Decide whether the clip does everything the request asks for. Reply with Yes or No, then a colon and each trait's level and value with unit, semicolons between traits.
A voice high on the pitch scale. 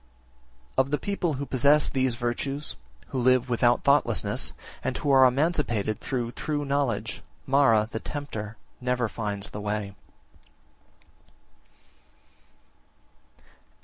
No: low, 130 Hz